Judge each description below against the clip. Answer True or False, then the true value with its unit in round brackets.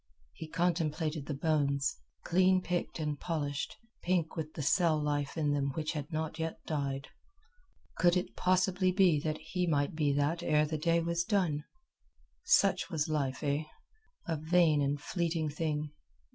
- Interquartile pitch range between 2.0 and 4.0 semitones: True (2.8 semitones)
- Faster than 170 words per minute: False (160 wpm)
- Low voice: False (155 Hz)